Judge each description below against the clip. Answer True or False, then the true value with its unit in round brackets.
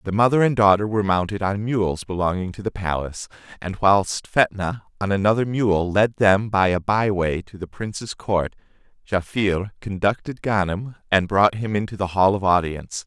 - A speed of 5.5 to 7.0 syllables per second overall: False (4.9 syllables/s)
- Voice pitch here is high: False (100 Hz)